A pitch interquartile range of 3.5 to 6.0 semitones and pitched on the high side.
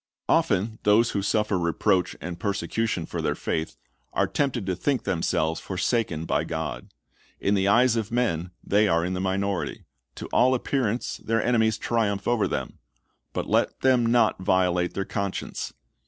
No: average, 4.2 semitones; low, 100 Hz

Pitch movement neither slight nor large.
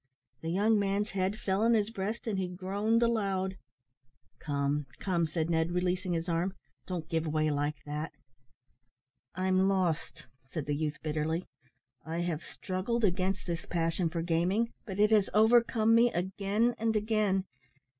Yes: average, 4.0 semitones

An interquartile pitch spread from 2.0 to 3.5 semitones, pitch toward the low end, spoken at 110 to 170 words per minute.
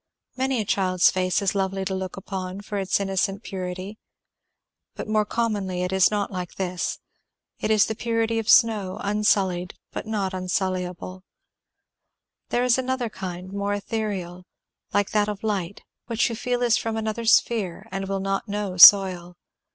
No: average, 2.8 semitones; high, 200 Hz; average, 160 wpm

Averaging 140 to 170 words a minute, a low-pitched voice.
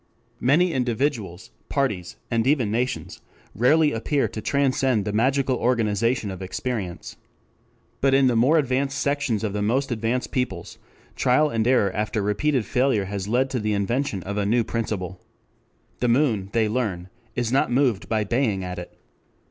Yes: average, 160 wpm; low, 115 Hz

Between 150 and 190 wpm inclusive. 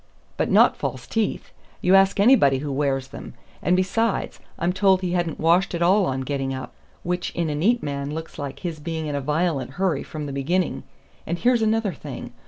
No: average, 200 wpm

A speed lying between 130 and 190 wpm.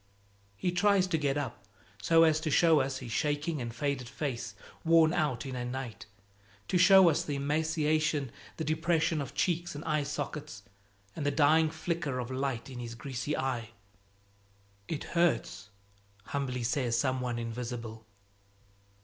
Yes: average, 155 wpm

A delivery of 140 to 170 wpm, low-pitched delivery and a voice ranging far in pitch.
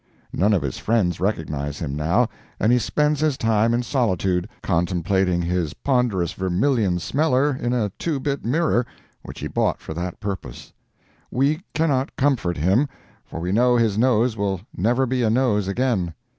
Yes: average, 165 wpm; low, 110 Hz; wide, 6.3 semitones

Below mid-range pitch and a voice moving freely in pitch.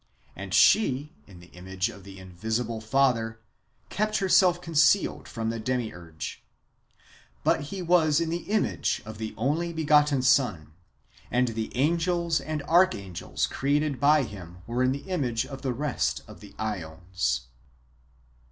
Yes: low, 130 Hz; wide, 6.9 semitones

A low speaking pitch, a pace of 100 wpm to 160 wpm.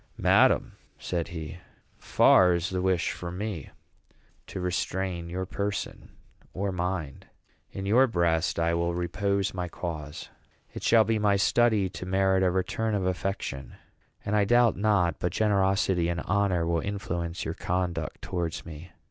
Yes: very low, 90 Hz; average, 150 wpm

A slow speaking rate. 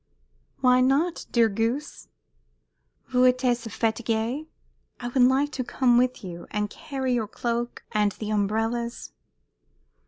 Yes: slow, 125 wpm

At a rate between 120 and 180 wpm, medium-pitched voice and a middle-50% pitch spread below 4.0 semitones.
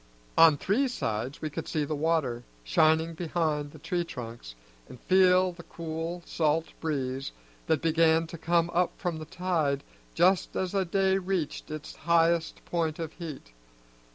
Yes: average, 155 wpm; medium, 165 Hz; narrow, 2.5 semitones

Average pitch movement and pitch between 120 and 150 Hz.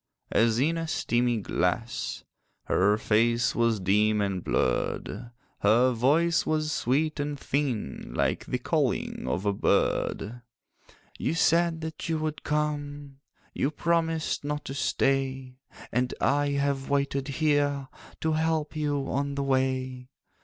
Yes: average, 4.2 semitones; low, 135 Hz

